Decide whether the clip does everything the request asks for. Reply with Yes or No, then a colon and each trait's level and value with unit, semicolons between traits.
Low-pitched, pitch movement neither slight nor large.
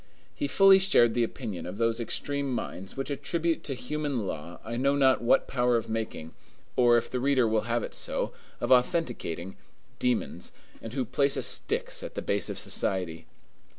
Yes: low, 120 Hz; average, 4.0 semitones